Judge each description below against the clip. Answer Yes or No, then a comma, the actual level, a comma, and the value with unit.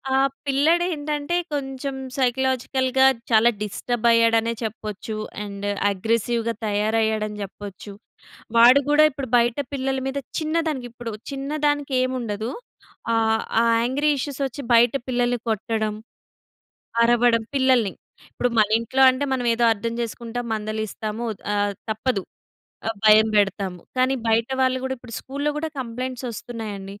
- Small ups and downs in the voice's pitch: No, average, 3.3 semitones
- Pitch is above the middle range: Yes, high, 240 Hz